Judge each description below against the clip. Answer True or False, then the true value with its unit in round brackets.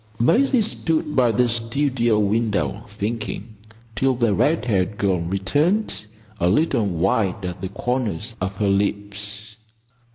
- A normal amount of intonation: True (4.0 semitones)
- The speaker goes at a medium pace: False (130 wpm)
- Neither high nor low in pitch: False (110 Hz)